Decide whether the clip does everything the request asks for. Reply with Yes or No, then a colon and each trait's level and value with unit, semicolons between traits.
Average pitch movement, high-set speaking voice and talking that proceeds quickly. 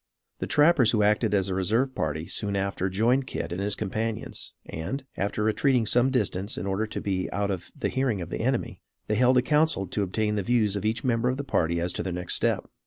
No: average, 4.5 semitones; low, 105 Hz; fast, 235 wpm